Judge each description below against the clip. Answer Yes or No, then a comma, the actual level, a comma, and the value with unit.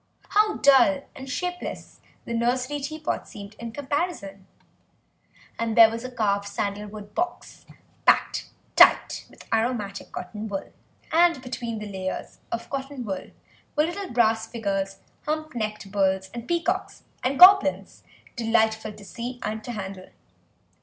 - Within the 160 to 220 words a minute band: No, average, 140 wpm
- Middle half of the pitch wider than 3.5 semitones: Yes, wide, 5.4 semitones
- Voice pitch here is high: Yes, high, 230 Hz